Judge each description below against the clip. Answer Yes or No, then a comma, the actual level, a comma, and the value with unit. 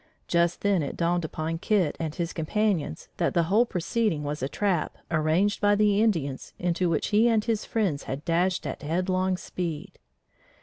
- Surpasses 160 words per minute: Yes, average, 175 wpm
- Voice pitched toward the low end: No, medium, 175 Hz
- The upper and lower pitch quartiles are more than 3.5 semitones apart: Yes, average, 4.4 semitones